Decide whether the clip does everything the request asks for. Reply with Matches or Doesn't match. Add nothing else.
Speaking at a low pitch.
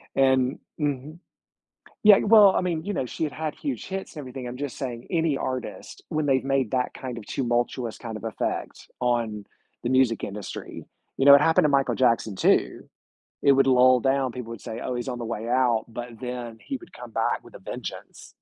Matches